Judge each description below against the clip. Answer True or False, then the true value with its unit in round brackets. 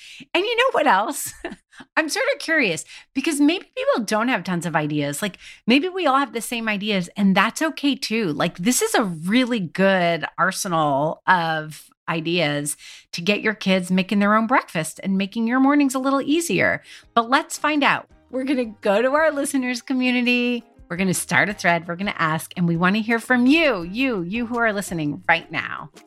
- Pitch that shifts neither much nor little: False (7.3 semitones)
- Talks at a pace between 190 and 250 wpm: True (205 wpm)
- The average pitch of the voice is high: True (220 Hz)